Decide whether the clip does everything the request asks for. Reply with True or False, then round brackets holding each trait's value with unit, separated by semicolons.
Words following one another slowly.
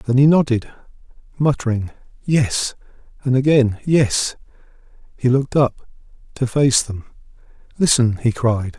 True (115 wpm)